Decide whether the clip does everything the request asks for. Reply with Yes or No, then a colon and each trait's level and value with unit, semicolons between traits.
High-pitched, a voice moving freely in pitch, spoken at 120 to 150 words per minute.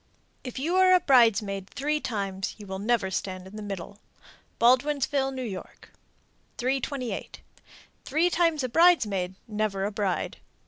Yes: high, 235 Hz; wide, 6.1 semitones; slow, 135 wpm